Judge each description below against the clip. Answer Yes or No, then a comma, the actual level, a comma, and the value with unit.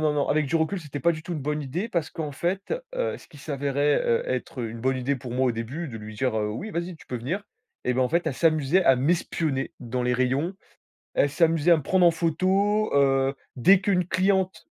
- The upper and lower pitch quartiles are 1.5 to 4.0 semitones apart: No, average, 4.9 semitones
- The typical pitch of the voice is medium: Yes, medium, 150 Hz